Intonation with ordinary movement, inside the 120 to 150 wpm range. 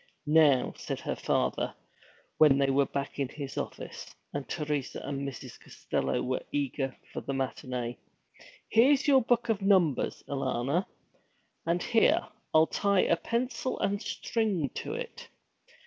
No: wide, 7.0 semitones; average, 145 wpm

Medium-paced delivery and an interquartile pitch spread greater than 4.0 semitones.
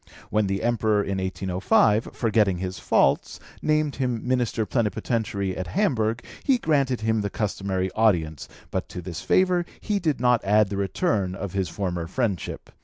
Yes: average, 160 wpm; average, 4.4 semitones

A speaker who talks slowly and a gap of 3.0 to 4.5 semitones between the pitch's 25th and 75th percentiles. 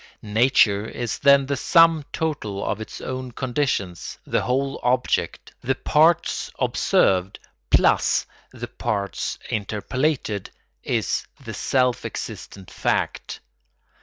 No: slow, 105 wpm; average, 5.1 semitones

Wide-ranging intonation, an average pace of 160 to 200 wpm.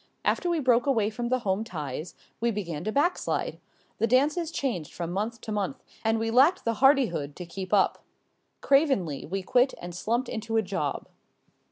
Yes: wide, 5.8 semitones; average, 185 wpm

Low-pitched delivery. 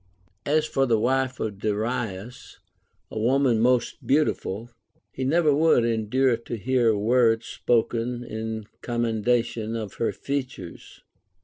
Yes: low, 120 Hz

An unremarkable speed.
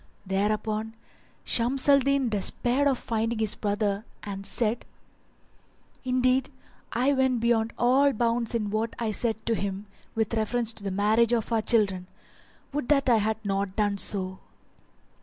Yes: average, 150 wpm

